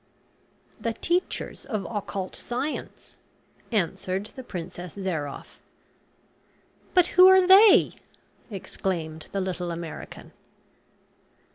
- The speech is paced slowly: Yes, slow, 90 wpm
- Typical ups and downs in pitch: No, wide, 7.0 semitones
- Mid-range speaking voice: No, high, 195 Hz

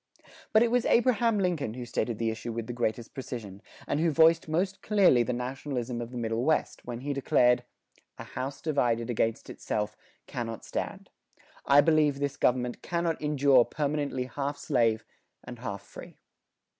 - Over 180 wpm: No, average, 165 wpm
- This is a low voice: Yes, low, 130 Hz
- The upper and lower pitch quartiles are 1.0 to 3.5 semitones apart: No, average, 4.5 semitones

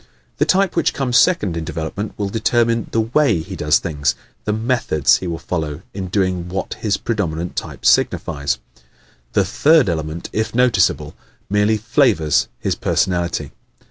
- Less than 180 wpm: Yes, average, 150 wpm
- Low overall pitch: Yes, very low, 95 Hz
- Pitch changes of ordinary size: No, wide, 6.0 semitones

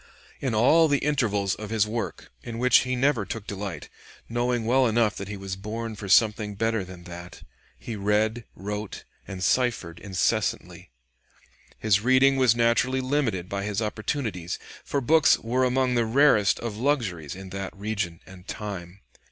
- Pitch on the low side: Yes, low, 110 Hz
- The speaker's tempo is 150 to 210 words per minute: Yes, average, 160 wpm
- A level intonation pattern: No, average, 4.1 semitones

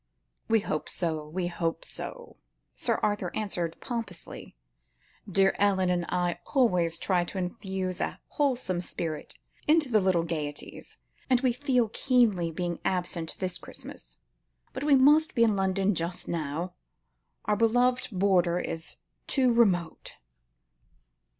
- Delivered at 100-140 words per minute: Yes, slow, 135 wpm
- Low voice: No, medium, 185 Hz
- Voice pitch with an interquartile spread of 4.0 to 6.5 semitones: Yes, average, 5.2 semitones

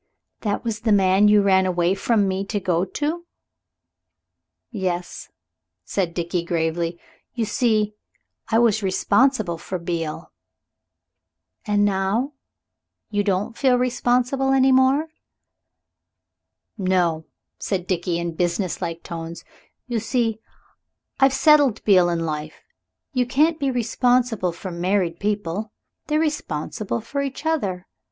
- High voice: Yes, high, 205 Hz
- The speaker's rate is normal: No, slow, 120 wpm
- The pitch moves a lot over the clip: Yes, wide, 5.8 semitones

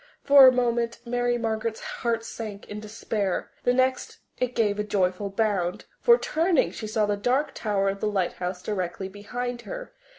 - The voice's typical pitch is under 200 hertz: No, high, 220 Hz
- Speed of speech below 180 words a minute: Yes, average, 170 wpm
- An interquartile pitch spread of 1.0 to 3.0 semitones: No, average, 3.4 semitones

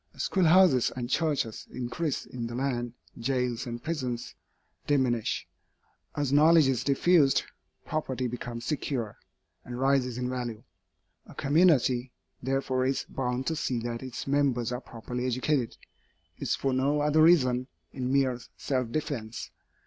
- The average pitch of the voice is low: Yes, low, 130 Hz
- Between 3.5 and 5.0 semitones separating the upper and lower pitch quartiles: No, average, 2.8 semitones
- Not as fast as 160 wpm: Yes, slow, 135 wpm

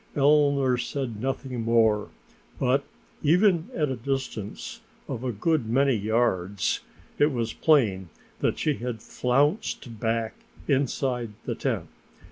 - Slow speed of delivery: Yes, slow, 120 wpm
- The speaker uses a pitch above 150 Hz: No, low, 125 Hz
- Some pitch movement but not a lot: Yes, average, 4.1 semitones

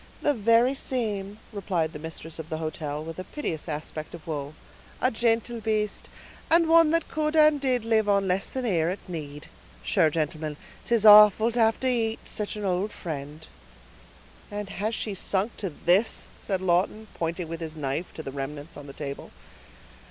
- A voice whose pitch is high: Yes, high, 195 Hz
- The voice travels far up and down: Yes, wide, 6.1 semitones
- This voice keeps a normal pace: Yes, average, 180 wpm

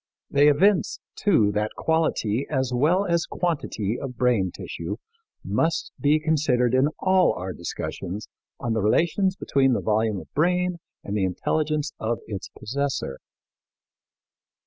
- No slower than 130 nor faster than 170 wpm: Yes, slow, 135 wpm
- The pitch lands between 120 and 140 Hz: Yes, low, 135 Hz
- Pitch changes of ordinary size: No, wide, 6.9 semitones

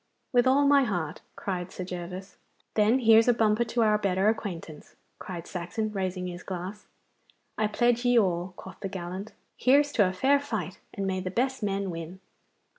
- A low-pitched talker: No, high, 200 Hz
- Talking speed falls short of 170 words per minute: No, average, 180 wpm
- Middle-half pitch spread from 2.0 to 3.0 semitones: No, average, 4.2 semitones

